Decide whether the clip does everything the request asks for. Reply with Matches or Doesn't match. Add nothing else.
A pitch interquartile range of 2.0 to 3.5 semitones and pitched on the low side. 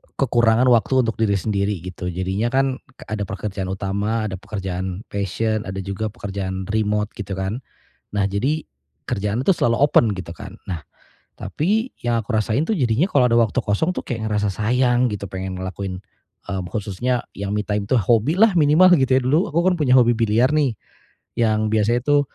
Doesn't match